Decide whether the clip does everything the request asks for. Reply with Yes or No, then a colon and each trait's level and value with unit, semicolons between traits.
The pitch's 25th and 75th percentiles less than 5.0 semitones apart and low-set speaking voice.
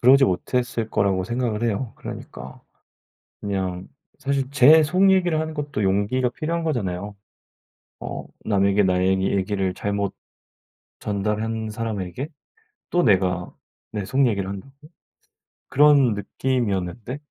No: wide, 5.4 semitones; low, 110 Hz